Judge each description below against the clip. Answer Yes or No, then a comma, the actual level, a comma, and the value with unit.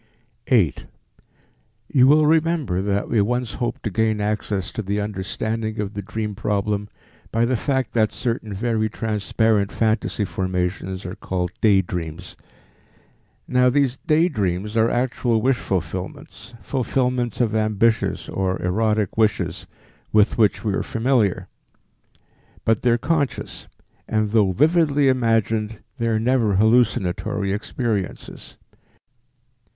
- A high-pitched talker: No, low, 110 Hz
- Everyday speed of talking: No, slow, 125 wpm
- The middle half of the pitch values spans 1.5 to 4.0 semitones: Yes, average, 3.4 semitones